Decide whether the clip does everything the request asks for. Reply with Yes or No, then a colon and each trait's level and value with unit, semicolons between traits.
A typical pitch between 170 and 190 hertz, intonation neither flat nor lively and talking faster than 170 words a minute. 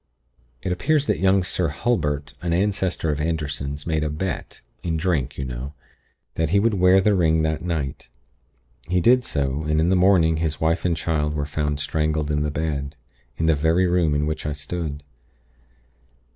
No: very low, 80 Hz; average, 3.3 semitones; average, 185 wpm